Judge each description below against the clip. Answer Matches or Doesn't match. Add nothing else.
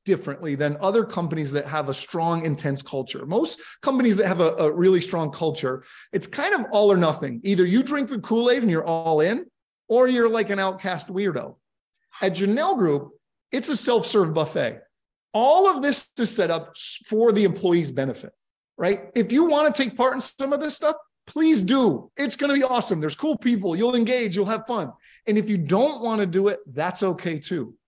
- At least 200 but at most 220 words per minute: Matches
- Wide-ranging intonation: Matches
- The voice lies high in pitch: Matches